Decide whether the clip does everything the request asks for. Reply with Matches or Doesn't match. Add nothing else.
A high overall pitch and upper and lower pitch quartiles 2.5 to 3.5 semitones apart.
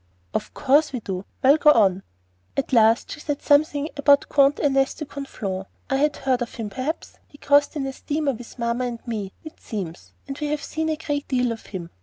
Doesn't match